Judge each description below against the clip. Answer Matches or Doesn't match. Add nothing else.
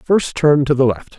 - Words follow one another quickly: Matches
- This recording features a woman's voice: Doesn't match